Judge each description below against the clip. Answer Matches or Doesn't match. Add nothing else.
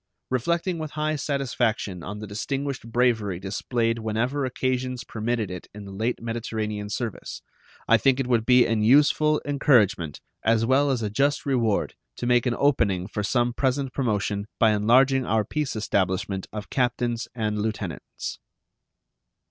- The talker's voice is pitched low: Matches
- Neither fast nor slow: Matches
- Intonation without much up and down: Doesn't match